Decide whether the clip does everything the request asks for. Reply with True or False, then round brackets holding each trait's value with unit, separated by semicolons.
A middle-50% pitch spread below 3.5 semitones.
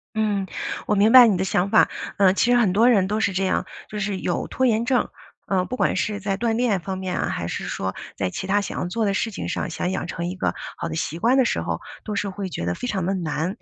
True (2.9 semitones)